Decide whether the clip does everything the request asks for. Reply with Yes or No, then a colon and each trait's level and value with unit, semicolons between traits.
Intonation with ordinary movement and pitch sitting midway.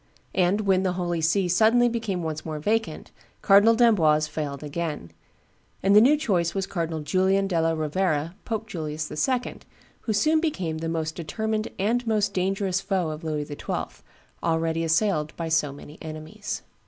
Yes: average, 4.7 semitones; medium, 175 Hz